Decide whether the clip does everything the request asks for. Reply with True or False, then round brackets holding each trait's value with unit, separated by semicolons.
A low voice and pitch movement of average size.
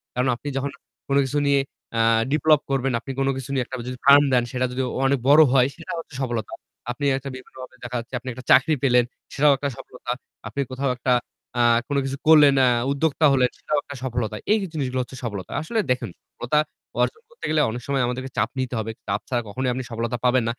False (130 Hz; 2.3 semitones)